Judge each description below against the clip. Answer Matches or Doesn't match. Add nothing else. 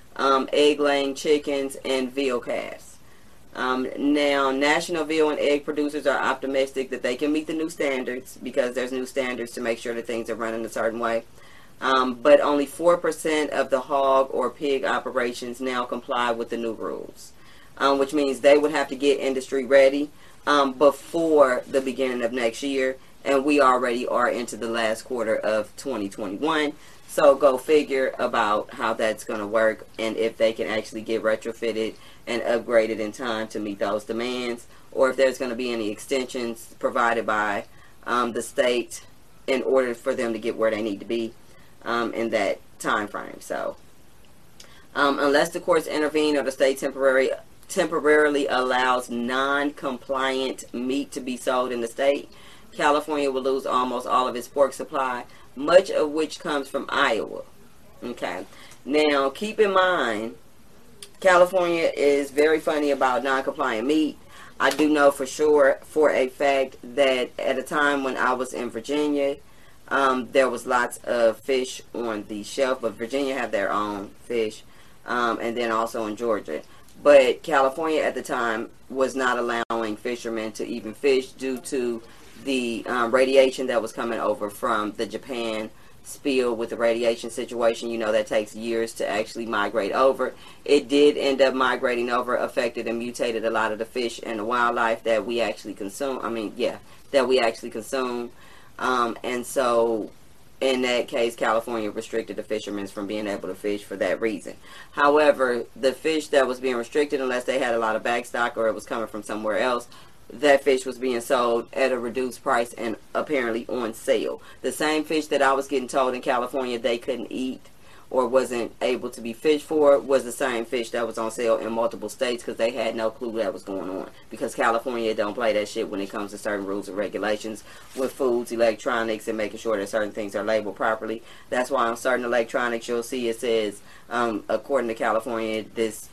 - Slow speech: Doesn't match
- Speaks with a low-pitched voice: Matches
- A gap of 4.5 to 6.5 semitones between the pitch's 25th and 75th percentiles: Doesn't match